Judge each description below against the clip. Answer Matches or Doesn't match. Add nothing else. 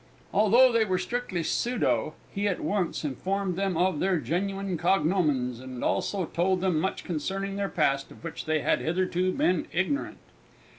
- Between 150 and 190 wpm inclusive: Matches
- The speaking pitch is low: Doesn't match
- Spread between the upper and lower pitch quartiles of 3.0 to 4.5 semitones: Matches